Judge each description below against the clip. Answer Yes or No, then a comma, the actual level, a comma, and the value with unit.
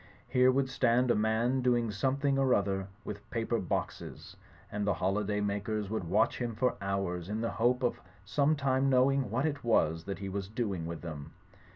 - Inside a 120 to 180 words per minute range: No, average, 195 wpm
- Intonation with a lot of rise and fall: No, average, 4.5 semitones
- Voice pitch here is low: Yes, low, 110 Hz